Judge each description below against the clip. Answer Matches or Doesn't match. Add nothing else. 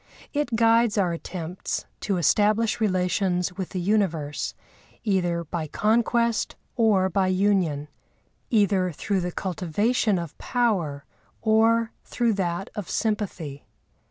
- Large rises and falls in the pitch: Doesn't match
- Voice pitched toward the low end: Doesn't match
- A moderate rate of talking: Doesn't match